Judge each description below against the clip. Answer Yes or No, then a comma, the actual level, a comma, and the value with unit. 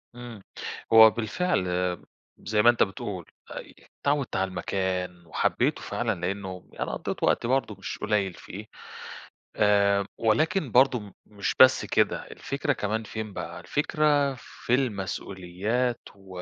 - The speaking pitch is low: Yes, low, 105 Hz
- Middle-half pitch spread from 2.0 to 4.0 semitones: No, average, 4.5 semitones